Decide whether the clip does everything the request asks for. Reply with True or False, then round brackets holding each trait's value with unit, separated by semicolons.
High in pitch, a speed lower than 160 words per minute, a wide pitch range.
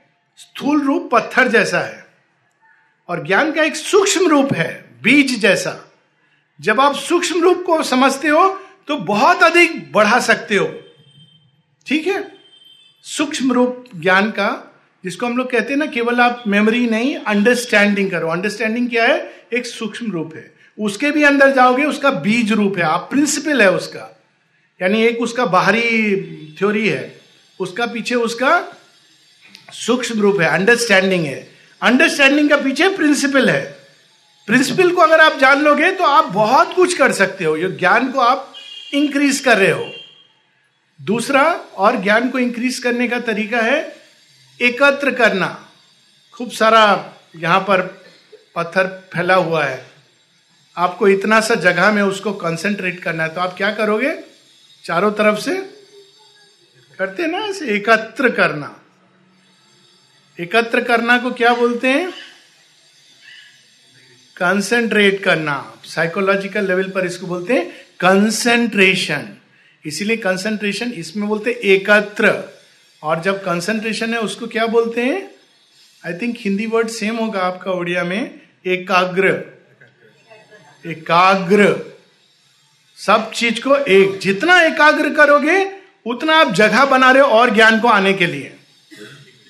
True (220 Hz; 135 wpm; 6.5 semitones)